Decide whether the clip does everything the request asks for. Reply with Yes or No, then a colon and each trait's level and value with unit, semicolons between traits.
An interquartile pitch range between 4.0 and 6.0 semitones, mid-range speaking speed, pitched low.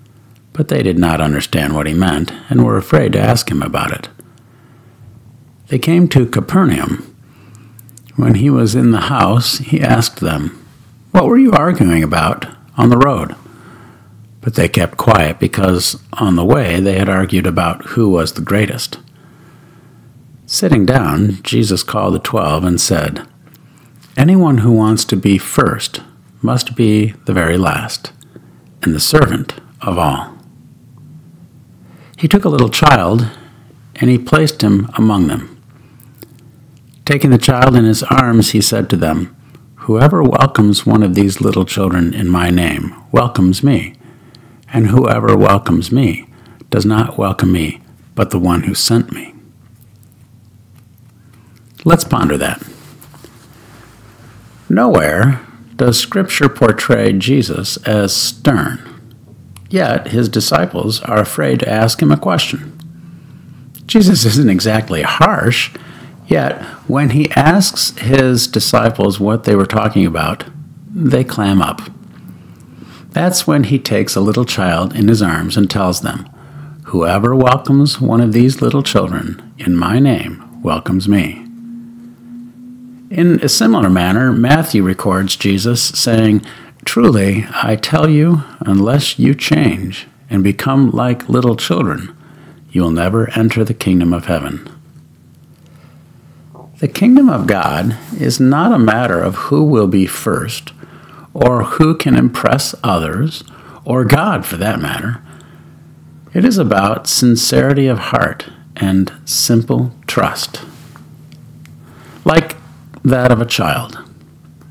No: wide, 5.4 semitones; slow, 130 wpm; low, 120 Hz